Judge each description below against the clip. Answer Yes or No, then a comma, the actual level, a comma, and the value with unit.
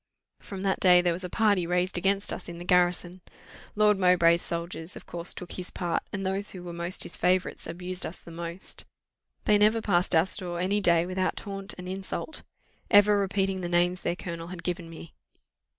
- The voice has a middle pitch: Yes, medium, 180 Hz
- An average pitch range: No, narrow, 1.9 semitones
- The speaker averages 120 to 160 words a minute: No, average, 200 wpm